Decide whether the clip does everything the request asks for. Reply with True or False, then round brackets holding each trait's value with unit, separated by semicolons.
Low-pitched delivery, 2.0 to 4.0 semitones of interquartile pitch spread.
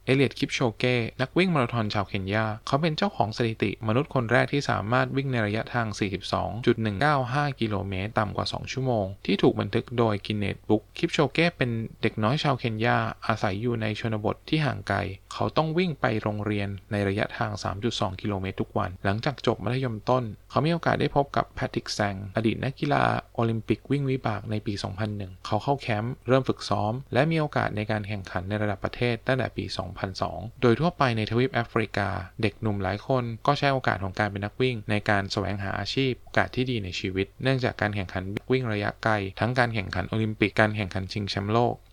True (110 Hz; 3.7 semitones)